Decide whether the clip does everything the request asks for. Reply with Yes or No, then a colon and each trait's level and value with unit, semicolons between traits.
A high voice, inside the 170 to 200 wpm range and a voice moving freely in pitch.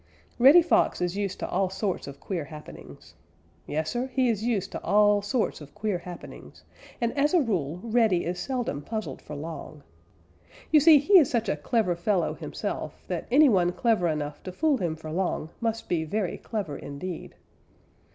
Yes: high, 195 Hz; average, 185 wpm; wide, 6.0 semitones